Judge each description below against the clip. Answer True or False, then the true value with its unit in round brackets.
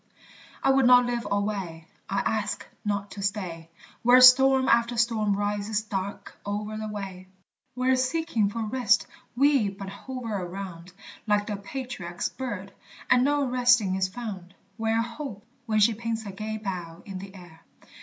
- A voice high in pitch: True (210 Hz)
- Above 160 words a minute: False (155 wpm)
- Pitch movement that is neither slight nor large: True (3.7 semitones)